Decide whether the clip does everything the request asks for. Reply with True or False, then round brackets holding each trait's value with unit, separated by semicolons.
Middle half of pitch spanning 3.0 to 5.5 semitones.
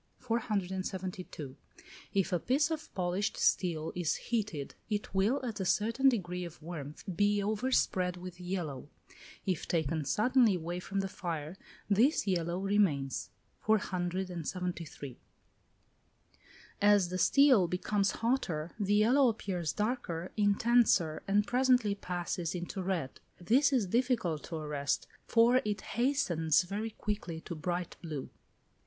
True (4.0 semitones)